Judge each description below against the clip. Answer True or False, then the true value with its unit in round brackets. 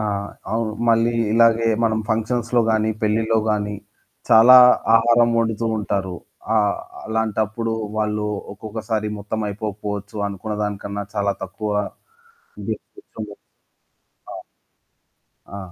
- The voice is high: False (110 Hz)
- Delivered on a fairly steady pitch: True (1.6 semitones)